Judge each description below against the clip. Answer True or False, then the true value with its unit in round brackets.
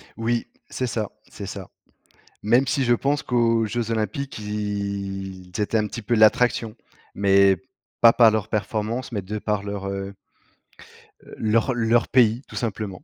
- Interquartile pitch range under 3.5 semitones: True (2.6 semitones)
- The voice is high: False (110 Hz)